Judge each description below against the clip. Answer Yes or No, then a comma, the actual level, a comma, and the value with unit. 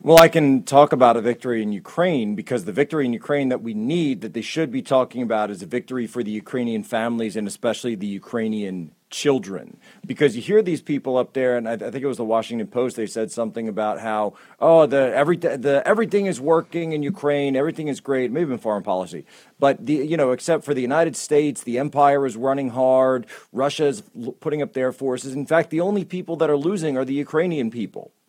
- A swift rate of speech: Yes, fast, 210 wpm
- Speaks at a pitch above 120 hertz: Yes, low, 135 Hz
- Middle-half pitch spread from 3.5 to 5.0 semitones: Yes, average, 4.5 semitones